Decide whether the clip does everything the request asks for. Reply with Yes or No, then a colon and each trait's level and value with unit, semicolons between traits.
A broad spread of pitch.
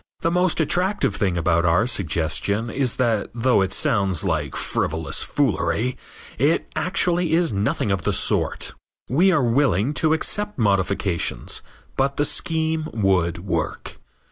Yes: wide, 8.8 semitones